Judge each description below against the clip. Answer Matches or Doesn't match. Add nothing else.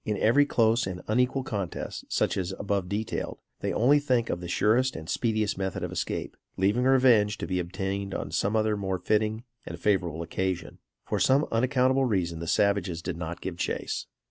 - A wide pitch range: Doesn't match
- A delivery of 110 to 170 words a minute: Doesn't match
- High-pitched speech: Doesn't match